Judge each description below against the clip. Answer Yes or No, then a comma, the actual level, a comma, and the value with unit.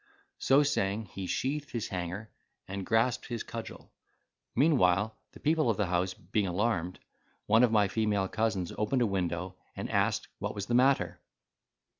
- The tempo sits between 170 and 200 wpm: No, average, 160 wpm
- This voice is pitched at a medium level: No, low, 105 Hz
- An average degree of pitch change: Yes, average, 4.3 semitones